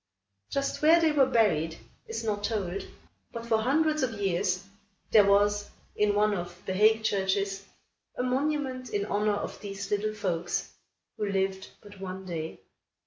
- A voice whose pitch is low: No, high, 205 Hz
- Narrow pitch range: No, average, 3.2 semitones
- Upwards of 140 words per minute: Yes, average, 155 wpm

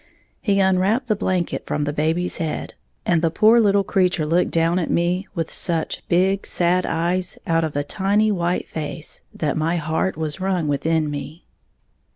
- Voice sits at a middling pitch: Yes, medium, 175 Hz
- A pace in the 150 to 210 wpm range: Yes, average, 175 wpm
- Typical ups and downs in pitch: Yes, average, 3.0 semitones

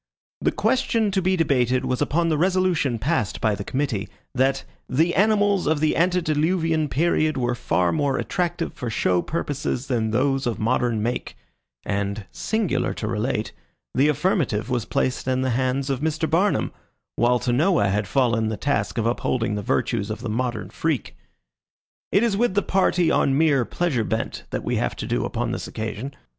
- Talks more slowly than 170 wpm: No, average, 175 wpm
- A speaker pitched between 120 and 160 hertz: Yes, low, 135 Hz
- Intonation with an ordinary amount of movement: No, wide, 6.1 semitones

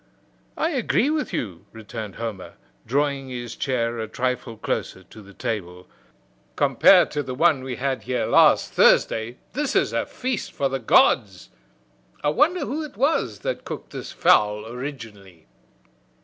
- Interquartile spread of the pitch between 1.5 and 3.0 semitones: No, average, 5.2 semitones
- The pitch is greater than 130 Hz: No, low, 125 Hz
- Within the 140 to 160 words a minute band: Yes, average, 150 wpm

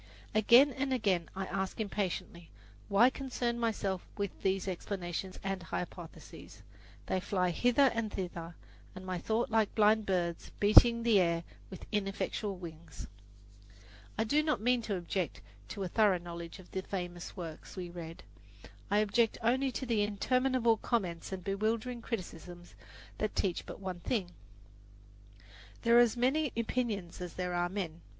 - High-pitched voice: Yes, high, 200 Hz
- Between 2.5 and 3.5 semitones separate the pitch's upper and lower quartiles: No, average, 4.5 semitones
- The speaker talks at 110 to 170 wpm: Yes, average, 150 wpm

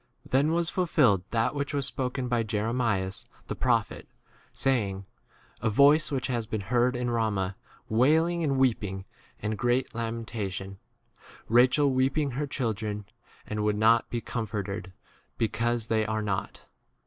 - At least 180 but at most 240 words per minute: No, average, 150 wpm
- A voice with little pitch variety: No, average, 3.7 semitones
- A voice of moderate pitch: No, low, 115 Hz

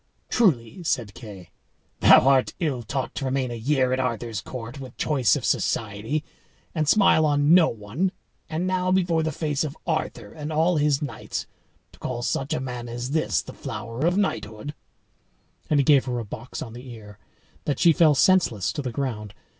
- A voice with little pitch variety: No, average, 5.0 semitones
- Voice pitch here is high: No, low, 135 Hz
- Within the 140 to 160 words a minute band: No, average, 185 wpm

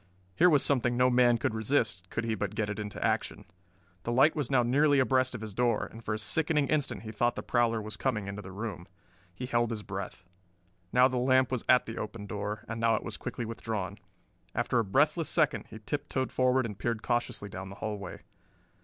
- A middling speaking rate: No, fast, 220 wpm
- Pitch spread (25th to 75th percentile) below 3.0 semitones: No, average, 3.4 semitones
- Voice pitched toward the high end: No, low, 115 Hz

